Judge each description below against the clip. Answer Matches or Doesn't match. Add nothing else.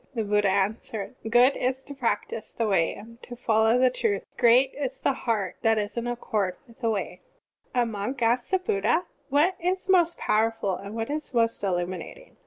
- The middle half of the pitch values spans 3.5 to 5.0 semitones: Matches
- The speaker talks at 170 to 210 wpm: Matches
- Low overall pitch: Doesn't match